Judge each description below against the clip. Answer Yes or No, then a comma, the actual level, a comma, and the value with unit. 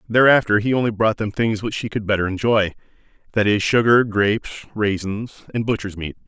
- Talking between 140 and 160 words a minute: No, average, 180 wpm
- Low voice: Yes, low, 110 Hz